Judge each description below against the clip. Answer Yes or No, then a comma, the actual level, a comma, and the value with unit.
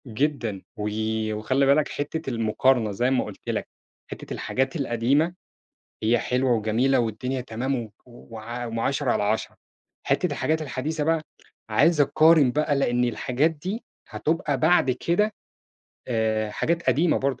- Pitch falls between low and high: No, low, 130 Hz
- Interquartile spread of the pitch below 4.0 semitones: No, average, 4.7 semitones